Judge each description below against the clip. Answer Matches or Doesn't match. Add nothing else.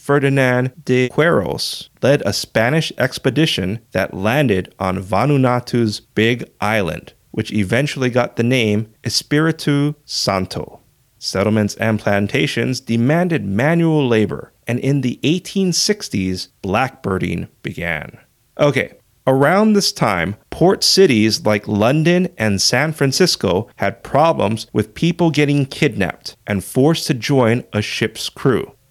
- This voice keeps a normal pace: Doesn't match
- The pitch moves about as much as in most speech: Doesn't match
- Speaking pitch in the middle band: Doesn't match